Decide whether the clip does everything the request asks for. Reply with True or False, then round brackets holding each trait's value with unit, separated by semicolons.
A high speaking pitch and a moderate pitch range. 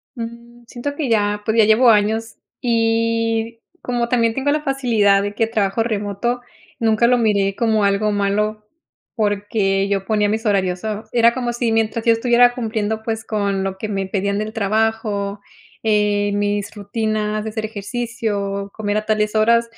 False (220 Hz; 2.1 semitones)